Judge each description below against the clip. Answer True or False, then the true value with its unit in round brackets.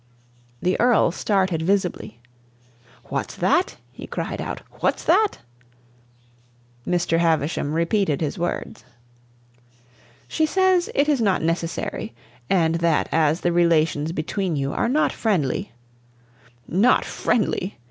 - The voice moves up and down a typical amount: True (4.6 semitones)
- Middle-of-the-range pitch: True (175 Hz)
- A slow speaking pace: True (115 wpm)